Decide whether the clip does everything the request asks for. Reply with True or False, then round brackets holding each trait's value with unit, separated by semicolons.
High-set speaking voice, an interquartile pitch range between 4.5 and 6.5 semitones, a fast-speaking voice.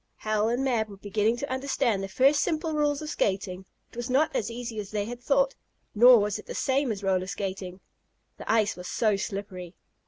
True (220 Hz; 4.8 semitones; 210 wpm)